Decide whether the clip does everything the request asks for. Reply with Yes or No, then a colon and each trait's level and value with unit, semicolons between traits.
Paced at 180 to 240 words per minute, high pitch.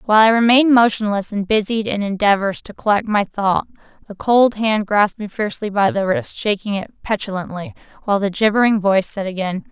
Yes: average, 185 wpm; high, 210 Hz